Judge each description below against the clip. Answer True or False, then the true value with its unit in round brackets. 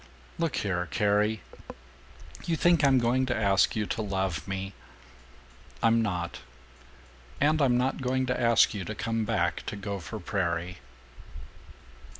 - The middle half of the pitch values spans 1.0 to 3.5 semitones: False (4.6 semitones)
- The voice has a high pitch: False (110 Hz)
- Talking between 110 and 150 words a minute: True (140 wpm)